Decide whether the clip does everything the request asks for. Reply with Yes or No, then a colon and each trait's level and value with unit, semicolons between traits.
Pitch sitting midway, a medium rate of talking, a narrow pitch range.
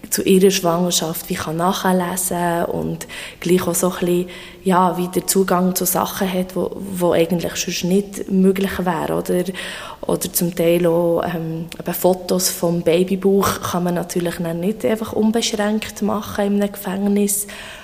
Yes: medium, 180 Hz; average, 150 wpm; narrow, 2.1 semitones